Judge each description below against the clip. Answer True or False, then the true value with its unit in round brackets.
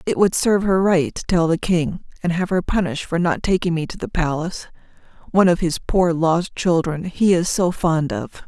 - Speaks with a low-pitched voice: False (170 Hz)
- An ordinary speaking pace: False (210 wpm)